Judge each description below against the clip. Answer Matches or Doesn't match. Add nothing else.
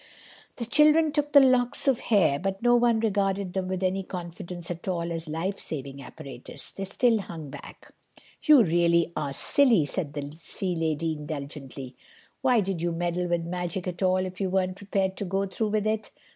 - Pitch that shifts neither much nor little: Matches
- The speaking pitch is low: Doesn't match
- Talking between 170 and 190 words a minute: Matches